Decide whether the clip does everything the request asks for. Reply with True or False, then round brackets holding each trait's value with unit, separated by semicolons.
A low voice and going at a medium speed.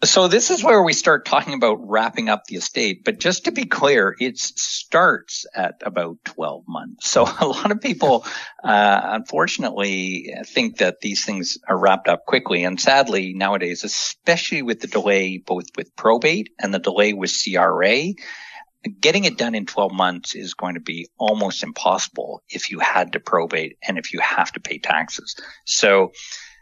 True (100 Hz; 175 wpm)